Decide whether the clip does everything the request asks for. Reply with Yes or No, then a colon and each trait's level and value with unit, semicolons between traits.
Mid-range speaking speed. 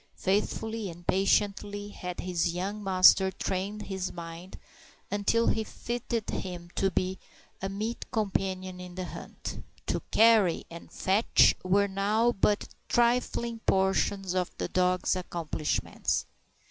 No: slow, 125 wpm